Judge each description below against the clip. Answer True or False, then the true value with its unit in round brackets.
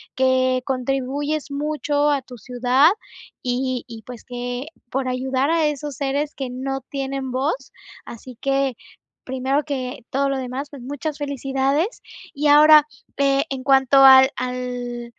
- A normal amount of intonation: False (1.9 semitones)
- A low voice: False (270 Hz)